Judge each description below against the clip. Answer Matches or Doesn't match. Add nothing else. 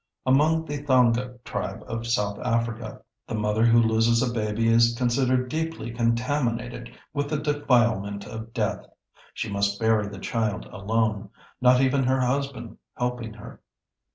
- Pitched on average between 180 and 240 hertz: Doesn't match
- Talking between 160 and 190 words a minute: Doesn't match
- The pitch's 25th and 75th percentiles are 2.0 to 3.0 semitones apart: Matches